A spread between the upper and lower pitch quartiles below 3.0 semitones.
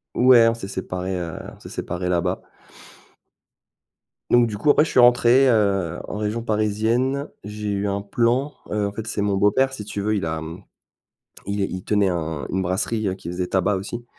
No: average, 3.6 semitones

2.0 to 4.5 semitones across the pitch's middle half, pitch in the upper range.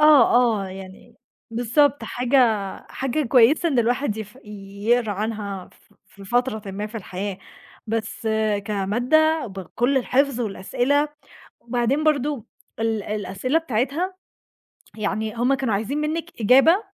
No: average, 5.0 semitones; high, 235 Hz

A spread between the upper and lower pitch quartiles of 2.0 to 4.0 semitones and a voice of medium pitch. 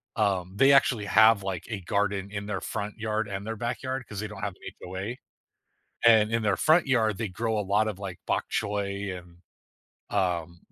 No: narrow, 2.4 semitones; low, 105 Hz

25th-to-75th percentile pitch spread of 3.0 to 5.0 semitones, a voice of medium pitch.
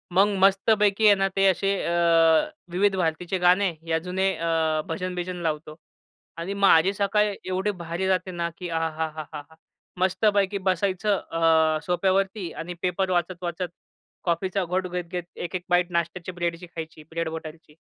No: narrow, 2.4 semitones; medium, 180 Hz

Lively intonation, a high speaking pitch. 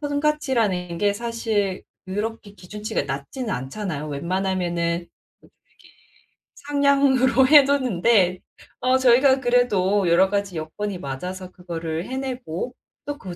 Yes: wide, 6.2 semitones; high, 205 Hz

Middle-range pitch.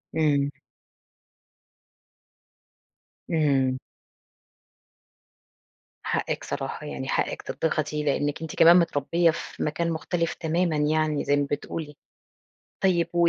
Yes: medium, 155 Hz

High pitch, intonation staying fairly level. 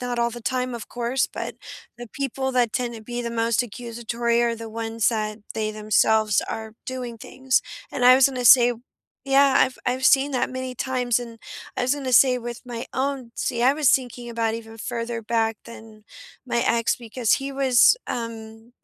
Yes: high, 240 Hz; narrow, 1.9 semitones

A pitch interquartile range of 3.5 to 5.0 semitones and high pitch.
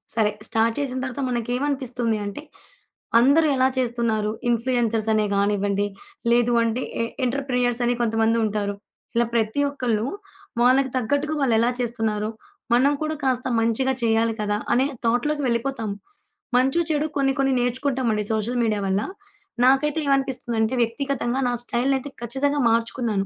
No: average, 3.1 semitones; high, 240 Hz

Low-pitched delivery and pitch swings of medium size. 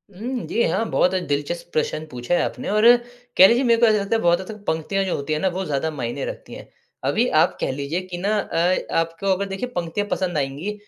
No: medium, 180 Hz; average, 4.7 semitones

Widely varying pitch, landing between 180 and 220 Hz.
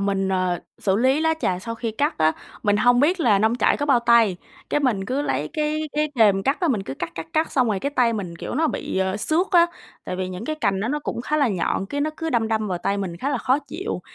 No: wide, 7.0 semitones; high, 230 Hz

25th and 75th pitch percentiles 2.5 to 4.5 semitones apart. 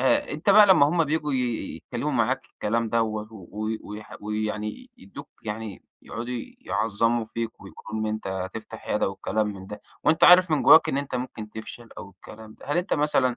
No: average, 5.3 semitones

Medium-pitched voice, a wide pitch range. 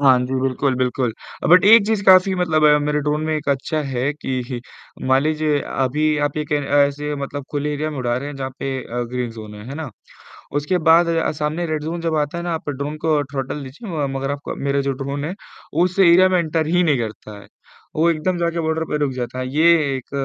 No: medium, 145 Hz; average, 3.2 semitones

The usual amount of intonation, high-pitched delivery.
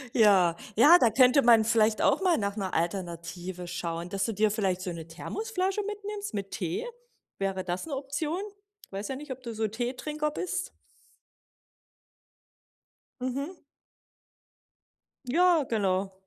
No: wide, 7.7 semitones; high, 220 Hz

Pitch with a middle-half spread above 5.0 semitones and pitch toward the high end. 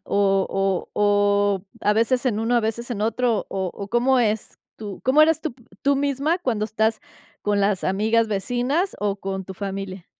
No: average, 3.7 semitones; high, 215 Hz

